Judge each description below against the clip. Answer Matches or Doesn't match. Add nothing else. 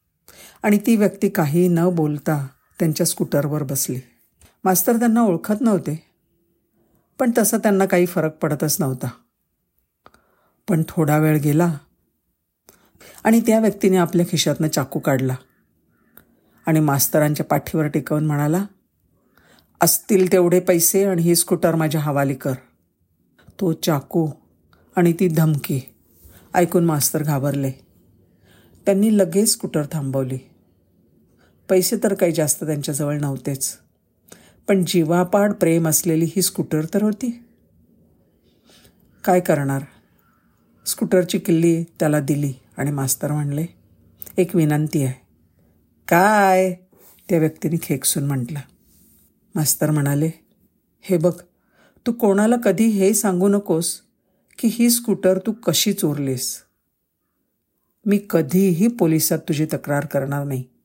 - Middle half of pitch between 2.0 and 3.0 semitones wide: Doesn't match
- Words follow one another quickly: Doesn't match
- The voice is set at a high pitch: Doesn't match